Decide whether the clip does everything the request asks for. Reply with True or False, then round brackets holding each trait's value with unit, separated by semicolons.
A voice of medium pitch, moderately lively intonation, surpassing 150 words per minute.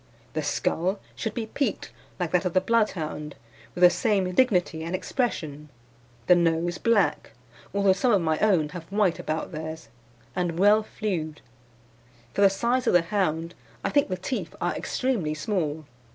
True (180 Hz; 4.7 semitones; 165 wpm)